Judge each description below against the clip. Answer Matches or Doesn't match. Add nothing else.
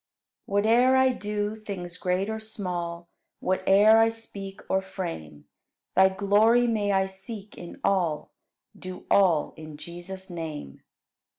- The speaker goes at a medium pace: Doesn't match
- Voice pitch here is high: Matches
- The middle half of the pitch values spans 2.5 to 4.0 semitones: Matches